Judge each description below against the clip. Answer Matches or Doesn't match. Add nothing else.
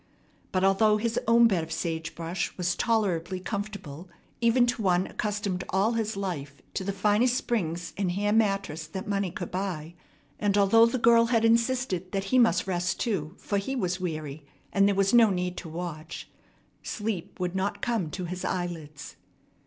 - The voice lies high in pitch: Matches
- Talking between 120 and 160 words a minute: Doesn't match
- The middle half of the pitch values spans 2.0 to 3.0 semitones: Doesn't match